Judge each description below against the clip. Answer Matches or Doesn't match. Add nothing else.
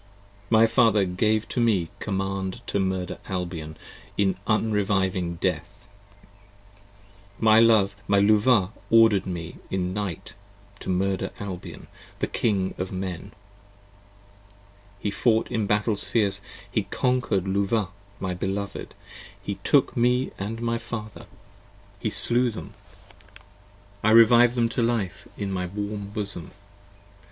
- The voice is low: Matches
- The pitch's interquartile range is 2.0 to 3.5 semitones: Matches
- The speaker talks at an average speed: Doesn't match